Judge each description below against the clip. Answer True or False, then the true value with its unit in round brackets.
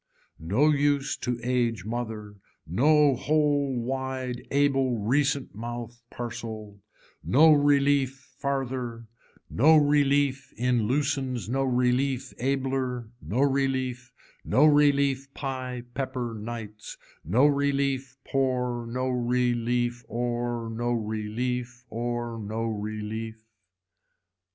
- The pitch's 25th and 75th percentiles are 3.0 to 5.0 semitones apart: False (2.6 semitones)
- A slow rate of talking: True (100 wpm)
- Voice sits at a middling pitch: False (125 Hz)